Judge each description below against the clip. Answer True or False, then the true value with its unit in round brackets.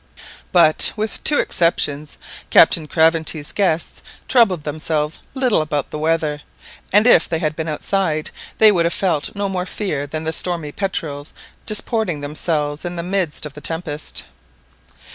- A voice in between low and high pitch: True (160 Hz)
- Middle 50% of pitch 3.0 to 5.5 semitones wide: True (3.6 semitones)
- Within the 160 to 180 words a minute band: False (150 wpm)